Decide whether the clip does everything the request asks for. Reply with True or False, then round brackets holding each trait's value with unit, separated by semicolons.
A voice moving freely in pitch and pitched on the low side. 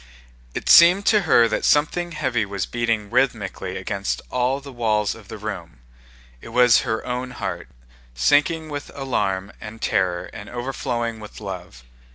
False (4.6 semitones; 115 Hz)